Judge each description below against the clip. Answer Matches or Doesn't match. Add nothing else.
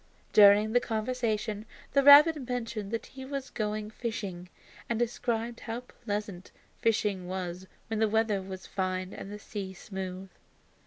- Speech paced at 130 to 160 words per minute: Matches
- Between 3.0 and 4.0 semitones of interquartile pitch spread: Matches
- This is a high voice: Matches